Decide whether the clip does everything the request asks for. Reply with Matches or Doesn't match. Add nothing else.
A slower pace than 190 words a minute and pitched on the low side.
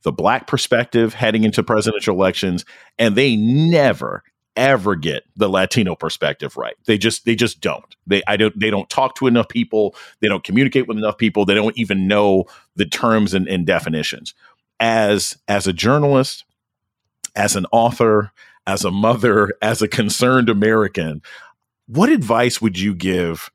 Matches